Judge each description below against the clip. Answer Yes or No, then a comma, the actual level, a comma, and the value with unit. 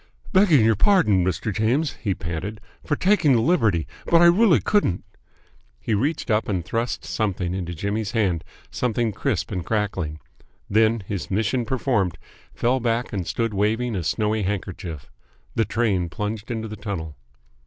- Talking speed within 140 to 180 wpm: Yes, average, 155 wpm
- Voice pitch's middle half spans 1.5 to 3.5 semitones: No, average, 4.1 semitones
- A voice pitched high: No, low, 110 Hz